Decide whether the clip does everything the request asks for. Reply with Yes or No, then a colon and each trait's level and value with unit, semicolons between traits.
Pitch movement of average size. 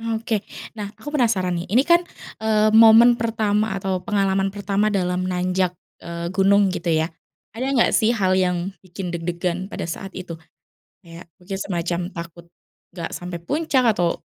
Yes: average, 3.5 semitones